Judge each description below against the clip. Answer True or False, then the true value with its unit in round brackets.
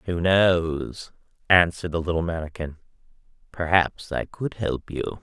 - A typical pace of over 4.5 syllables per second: False (4.3 syllables/s)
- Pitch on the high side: False (85 Hz)